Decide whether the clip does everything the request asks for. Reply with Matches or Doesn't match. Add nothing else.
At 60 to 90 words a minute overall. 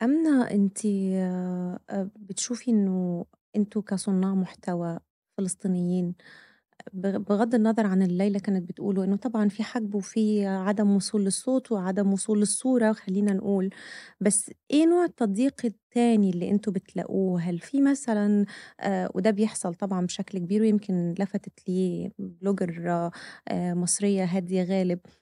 Doesn't match